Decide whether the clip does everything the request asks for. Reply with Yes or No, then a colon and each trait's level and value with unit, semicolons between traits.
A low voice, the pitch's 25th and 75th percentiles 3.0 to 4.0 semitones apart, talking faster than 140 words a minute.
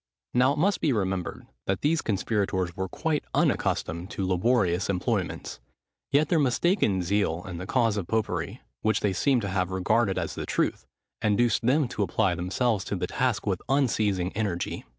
No: low, 105 Hz; average, 5.2 semitones; average, 170 wpm